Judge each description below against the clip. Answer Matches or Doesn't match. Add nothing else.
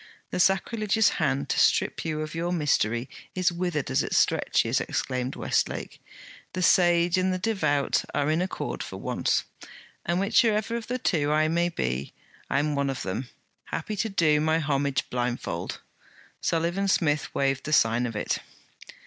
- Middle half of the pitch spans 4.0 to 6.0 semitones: Matches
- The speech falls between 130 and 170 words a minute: Matches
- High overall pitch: Doesn't match